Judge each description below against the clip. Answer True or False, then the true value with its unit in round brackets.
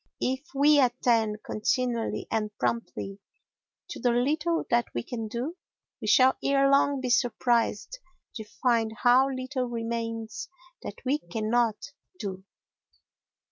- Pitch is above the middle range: True (240 Hz)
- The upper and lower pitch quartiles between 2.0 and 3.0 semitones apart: True (2.7 semitones)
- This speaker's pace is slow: True (125 wpm)